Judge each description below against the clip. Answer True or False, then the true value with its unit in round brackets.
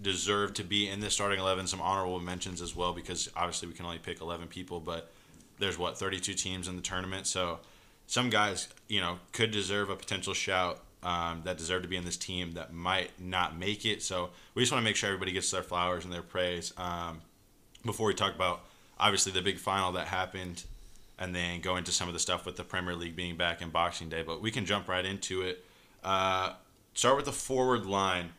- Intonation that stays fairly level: True (1.9 semitones)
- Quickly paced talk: True (225 wpm)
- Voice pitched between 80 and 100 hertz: True (90 Hz)